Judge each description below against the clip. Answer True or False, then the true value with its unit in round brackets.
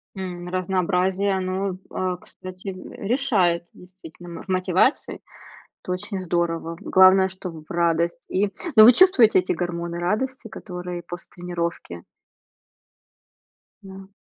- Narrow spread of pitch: True (1.8 semitones)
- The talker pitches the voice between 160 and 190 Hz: True (185 Hz)